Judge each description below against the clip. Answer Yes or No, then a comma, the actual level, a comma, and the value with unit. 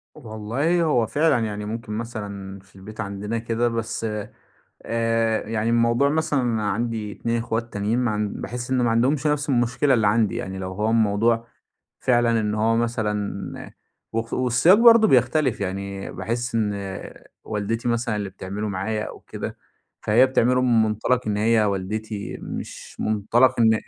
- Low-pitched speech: Yes, low, 115 Hz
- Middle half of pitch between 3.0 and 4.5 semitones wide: No, narrow, 2.4 semitones